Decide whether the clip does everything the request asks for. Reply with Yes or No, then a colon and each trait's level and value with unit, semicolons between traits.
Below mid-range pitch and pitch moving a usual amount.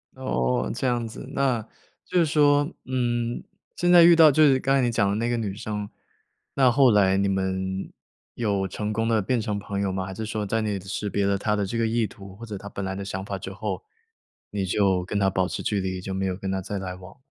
Yes: low, 105 Hz; average, 3.7 semitones